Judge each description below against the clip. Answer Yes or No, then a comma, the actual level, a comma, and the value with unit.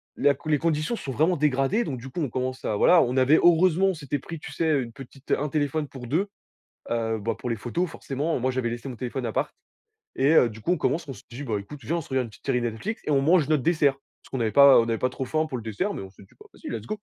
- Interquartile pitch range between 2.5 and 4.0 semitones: No, average, 4.4 semitones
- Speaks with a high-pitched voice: No, low, 135 Hz